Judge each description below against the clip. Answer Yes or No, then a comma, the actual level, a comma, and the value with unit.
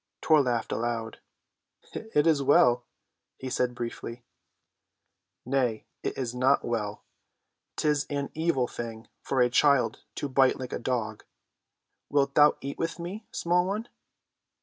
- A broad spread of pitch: No, average, 3.7 semitones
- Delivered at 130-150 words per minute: Yes, slow, 135 wpm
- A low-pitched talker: Yes, low, 130 Hz